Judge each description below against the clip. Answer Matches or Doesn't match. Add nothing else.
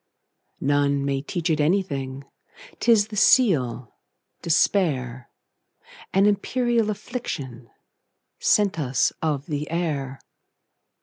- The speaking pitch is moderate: Matches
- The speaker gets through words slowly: Matches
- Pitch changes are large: Matches